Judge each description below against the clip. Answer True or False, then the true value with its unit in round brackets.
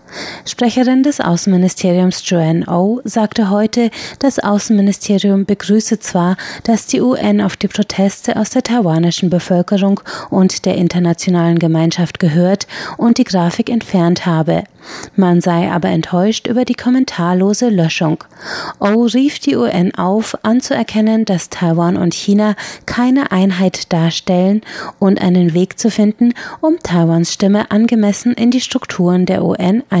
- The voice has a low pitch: False (200 Hz)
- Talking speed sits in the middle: True (140 wpm)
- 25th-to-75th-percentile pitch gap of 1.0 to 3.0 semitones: False (4.2 semitones)